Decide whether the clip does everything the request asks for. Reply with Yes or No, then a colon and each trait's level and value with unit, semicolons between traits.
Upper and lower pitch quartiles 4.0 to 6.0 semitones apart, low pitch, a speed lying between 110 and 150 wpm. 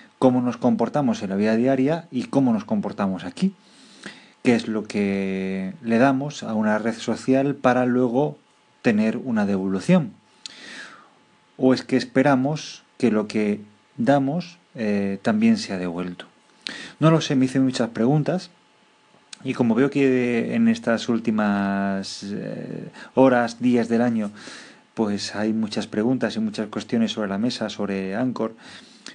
Yes: average, 4.4 semitones; low, 120 Hz; average, 140 wpm